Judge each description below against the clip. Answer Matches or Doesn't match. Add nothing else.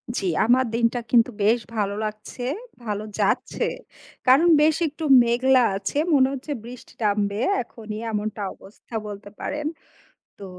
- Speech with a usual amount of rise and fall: Matches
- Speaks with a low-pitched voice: Doesn't match